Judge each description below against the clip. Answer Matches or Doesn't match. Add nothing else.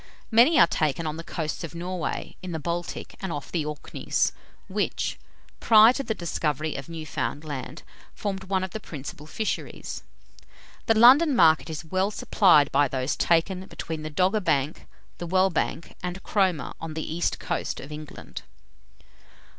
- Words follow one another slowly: Doesn't match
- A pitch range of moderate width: Matches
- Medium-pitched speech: Matches